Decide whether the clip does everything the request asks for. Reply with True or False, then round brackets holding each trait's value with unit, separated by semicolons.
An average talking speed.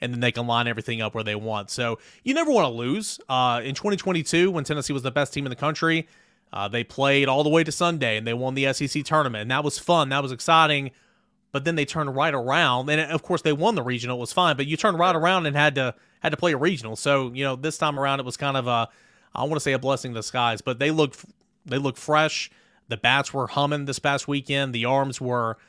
False (265 wpm)